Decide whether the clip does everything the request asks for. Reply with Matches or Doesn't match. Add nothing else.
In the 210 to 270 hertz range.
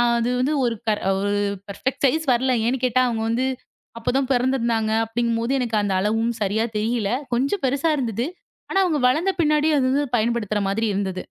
Matches